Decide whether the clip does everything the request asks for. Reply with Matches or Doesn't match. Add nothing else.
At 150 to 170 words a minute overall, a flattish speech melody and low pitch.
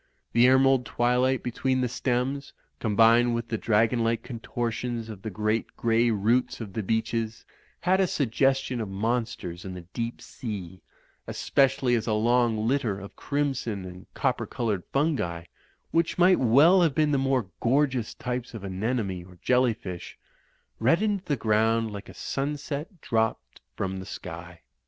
Doesn't match